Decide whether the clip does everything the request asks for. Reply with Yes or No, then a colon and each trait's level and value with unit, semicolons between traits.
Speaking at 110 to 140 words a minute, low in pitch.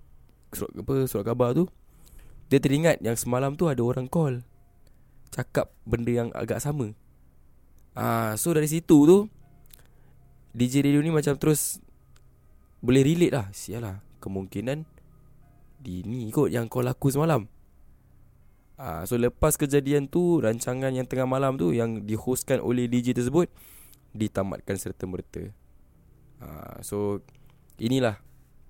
Yes: average, 130 wpm; low, 120 Hz